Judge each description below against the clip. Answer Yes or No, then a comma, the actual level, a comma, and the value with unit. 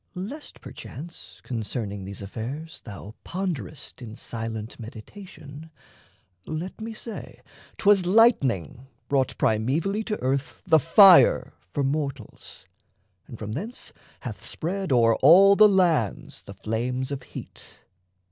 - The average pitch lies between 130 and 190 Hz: Yes, medium, 140 Hz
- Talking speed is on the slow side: Yes, slow, 120 wpm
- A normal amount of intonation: No, wide, 8.5 semitones